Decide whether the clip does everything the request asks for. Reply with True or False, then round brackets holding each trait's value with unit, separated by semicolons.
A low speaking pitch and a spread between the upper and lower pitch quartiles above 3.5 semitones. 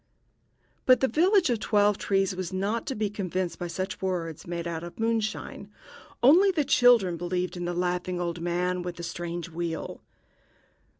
False (185 Hz; 4.0 semitones)